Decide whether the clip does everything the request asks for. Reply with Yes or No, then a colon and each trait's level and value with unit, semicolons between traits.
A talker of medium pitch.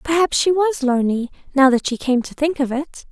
No: very high, 280 Hz